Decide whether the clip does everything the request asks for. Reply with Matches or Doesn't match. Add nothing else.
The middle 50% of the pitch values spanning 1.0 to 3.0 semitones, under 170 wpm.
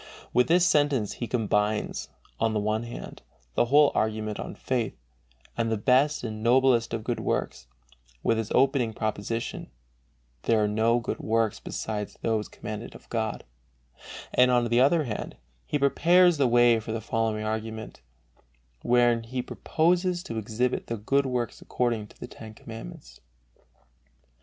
Matches